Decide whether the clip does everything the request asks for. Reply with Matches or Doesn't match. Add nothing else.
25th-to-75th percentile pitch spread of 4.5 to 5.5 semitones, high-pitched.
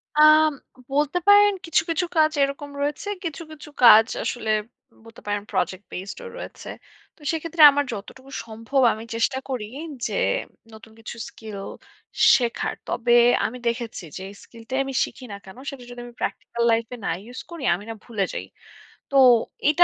Matches